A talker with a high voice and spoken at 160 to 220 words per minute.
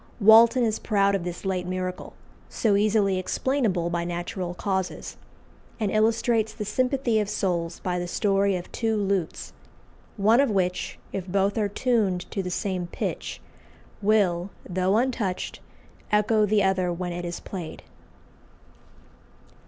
No: high, 195 Hz; average, 140 wpm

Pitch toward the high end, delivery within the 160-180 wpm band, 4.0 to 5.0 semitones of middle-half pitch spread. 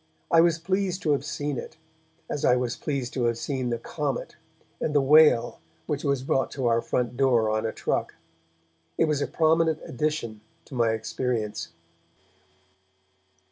No: low, 135 Hz; average, 165 wpm; average, 4.3 semitones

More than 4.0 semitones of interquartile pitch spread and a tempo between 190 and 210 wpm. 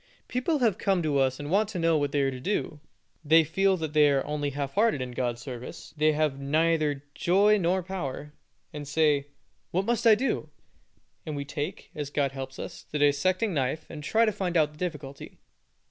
Yes: average, 4.5 semitones; average, 200 wpm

